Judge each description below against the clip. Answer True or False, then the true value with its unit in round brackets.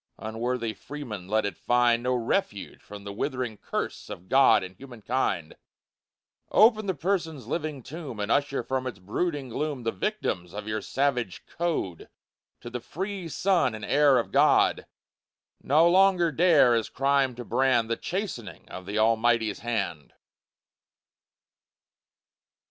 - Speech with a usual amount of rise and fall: False (5.7 semitones)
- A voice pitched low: True (125 Hz)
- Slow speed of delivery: False (145 wpm)